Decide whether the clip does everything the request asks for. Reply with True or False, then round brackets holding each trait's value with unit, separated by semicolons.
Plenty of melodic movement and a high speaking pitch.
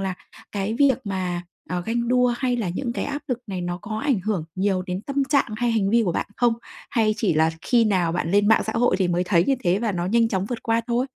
False (4.6 semitones; 215 Hz)